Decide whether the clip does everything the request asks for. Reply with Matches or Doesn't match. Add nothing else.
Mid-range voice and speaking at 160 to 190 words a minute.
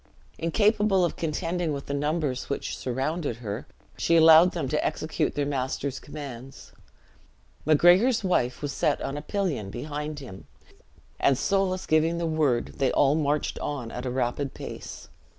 Doesn't match